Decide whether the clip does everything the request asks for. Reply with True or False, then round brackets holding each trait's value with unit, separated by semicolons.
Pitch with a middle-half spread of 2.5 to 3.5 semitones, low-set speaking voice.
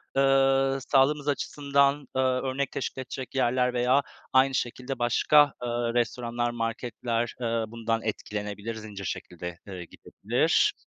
True (2.8 semitones; 125 Hz)